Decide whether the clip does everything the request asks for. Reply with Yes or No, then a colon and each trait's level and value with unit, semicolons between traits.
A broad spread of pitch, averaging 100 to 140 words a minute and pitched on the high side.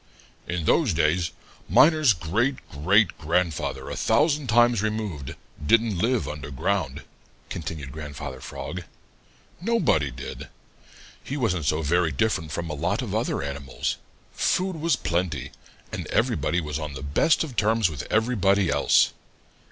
No: wide, 7.1 semitones; slow, 135 wpm; very low, 90 Hz